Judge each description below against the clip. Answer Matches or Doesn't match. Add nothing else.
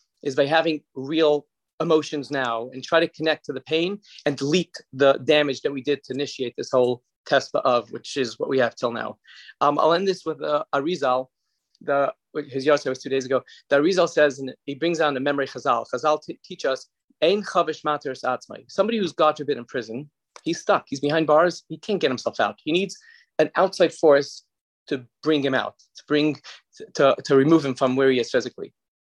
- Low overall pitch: Doesn't match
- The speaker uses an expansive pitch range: Doesn't match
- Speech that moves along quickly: Matches